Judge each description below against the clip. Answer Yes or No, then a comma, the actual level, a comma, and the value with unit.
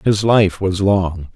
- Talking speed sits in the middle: Yes, average, 175 wpm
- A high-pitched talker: No, very low, 95 Hz